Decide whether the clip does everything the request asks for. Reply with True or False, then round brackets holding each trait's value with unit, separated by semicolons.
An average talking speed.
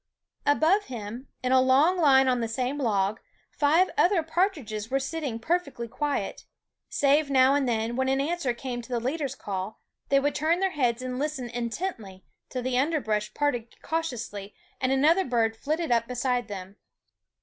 True (170 wpm)